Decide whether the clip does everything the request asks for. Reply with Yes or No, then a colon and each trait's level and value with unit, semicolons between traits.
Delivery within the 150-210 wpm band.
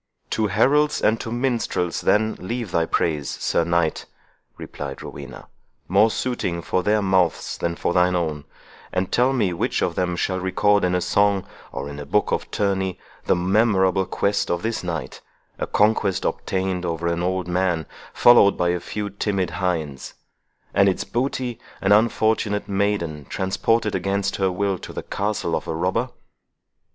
Yes: average, 160 wpm